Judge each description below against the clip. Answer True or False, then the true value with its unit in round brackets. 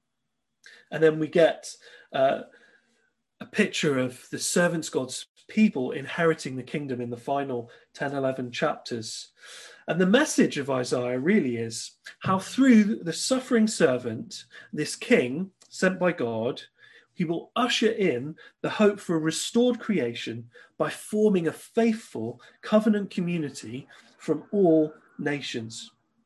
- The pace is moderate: False (130 wpm)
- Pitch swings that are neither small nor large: False (8.5 semitones)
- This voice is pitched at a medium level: True (160 Hz)